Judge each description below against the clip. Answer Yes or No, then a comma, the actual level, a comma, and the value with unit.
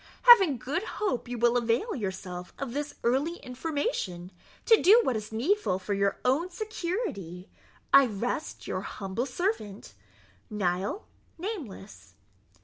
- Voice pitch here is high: Yes, high, 245 Hz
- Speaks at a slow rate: Yes, slow, 130 wpm